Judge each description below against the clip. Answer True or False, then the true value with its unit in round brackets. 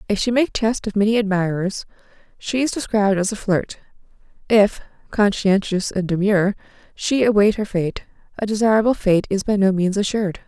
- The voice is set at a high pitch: True (205 Hz)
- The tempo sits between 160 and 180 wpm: True (165 wpm)